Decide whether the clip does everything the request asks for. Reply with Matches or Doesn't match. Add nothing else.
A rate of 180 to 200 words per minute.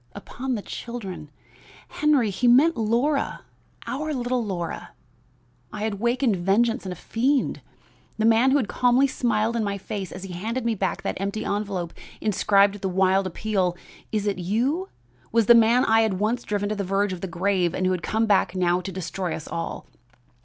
Matches